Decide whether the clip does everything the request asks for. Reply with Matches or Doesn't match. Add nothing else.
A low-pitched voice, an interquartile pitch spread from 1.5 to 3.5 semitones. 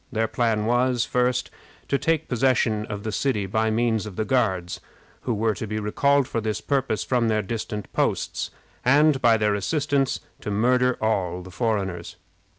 Matches